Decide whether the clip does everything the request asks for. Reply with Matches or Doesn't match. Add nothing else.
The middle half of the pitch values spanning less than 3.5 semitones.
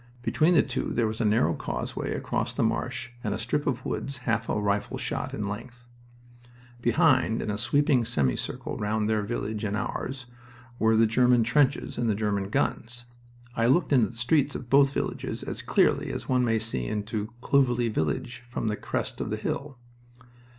Matches